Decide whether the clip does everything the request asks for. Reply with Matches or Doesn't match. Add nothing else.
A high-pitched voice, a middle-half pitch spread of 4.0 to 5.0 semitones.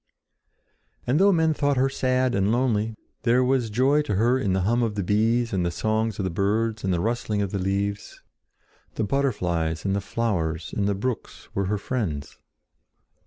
Doesn't match